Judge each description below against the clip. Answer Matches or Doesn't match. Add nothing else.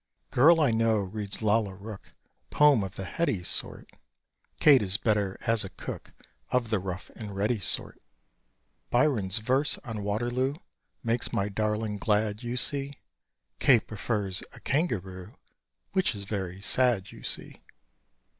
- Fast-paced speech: Doesn't match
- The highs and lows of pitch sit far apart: Doesn't match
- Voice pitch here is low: Matches